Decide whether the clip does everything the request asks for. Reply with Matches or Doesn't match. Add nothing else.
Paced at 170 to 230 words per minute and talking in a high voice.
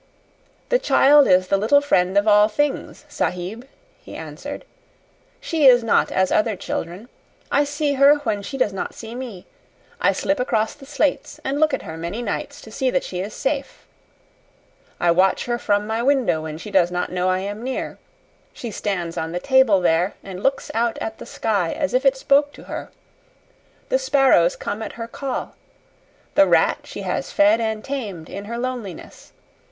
Matches